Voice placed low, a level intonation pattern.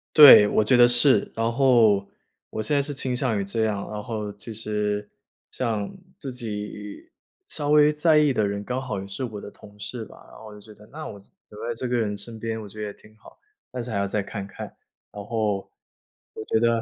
No: low, 110 Hz; average, 3.2 semitones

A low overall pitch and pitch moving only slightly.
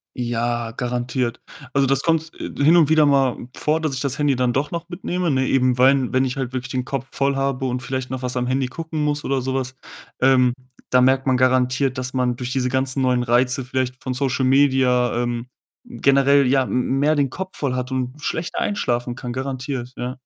Yes: low, 130 Hz; narrow, 1.7 semitones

